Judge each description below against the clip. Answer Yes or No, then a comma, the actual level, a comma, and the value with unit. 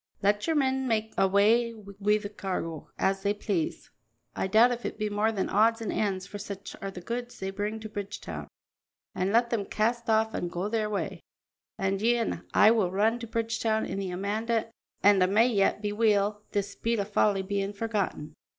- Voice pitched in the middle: No, high, 210 Hz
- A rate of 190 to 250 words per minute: Yes, average, 200 wpm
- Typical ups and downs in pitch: No, narrow, 2.3 semitones